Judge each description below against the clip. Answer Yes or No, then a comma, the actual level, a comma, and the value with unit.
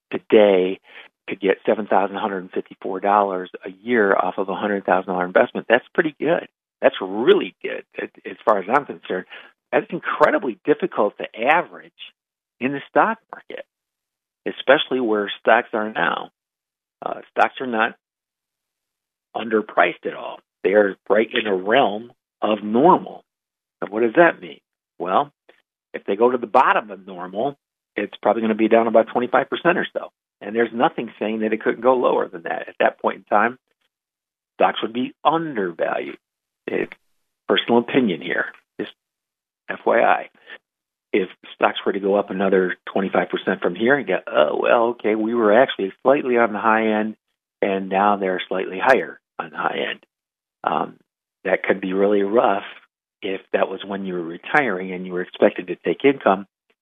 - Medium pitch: No, low, 110 Hz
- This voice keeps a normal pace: Yes, average, 170 wpm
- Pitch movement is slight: No, average, 4.0 semitones